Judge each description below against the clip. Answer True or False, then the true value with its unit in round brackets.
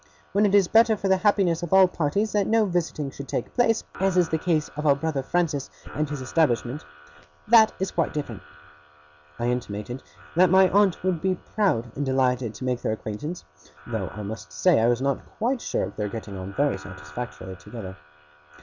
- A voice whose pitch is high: False (150 Hz)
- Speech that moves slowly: False (195 wpm)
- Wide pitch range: True (8.0 semitones)